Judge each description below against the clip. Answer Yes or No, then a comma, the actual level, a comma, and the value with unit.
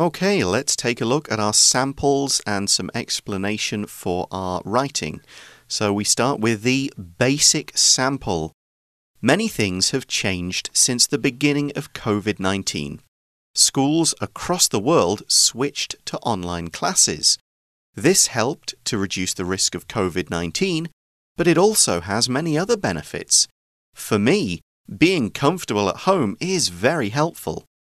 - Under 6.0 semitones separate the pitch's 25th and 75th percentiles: No, wide, 7.1 semitones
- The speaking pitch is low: Yes, low, 115 Hz